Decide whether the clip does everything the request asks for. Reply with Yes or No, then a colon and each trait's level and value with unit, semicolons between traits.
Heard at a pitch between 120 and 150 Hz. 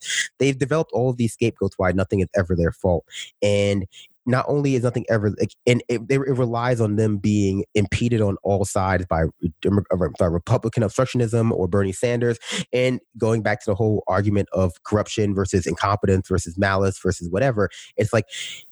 No: low, 105 Hz